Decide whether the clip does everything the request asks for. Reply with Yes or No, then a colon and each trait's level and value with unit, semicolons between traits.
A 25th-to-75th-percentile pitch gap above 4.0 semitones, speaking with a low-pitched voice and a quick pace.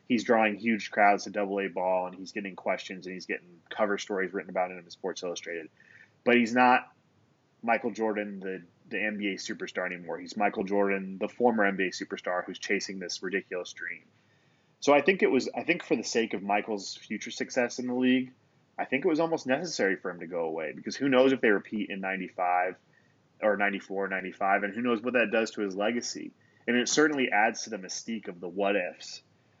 Yes: average, 4.5 semitones; low, 105 Hz; fast, 215 wpm